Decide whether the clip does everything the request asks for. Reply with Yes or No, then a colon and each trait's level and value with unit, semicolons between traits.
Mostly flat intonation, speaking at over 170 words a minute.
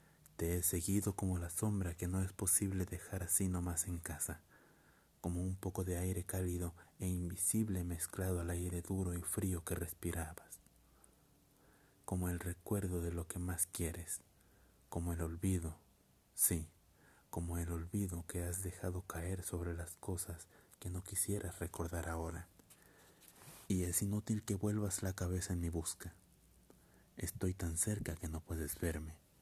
No: narrow, 1.6 semitones; average, 155 wpm